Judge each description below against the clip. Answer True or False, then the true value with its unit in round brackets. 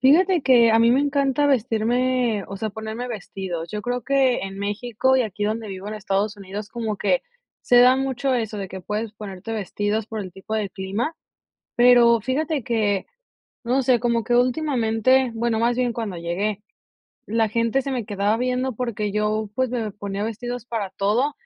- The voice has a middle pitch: False (225 Hz)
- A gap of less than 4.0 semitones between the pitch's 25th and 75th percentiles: True (3.3 semitones)